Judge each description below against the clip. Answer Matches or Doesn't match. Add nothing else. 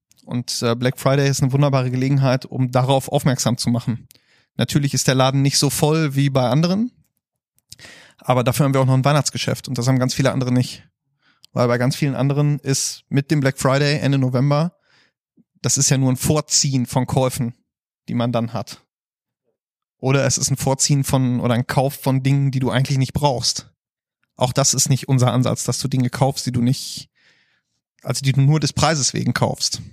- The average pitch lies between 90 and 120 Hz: Doesn't match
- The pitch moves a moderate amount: Doesn't match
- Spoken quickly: Matches